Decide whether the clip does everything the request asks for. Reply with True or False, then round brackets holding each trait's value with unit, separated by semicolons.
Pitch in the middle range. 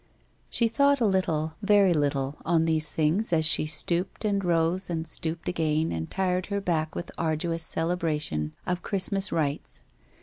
True (165 Hz)